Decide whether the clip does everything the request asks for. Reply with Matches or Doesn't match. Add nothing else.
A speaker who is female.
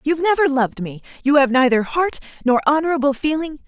Matches